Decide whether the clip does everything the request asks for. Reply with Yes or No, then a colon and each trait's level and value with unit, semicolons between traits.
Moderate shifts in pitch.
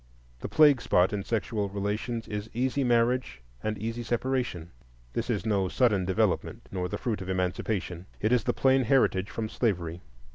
Yes: average, 4.3 semitones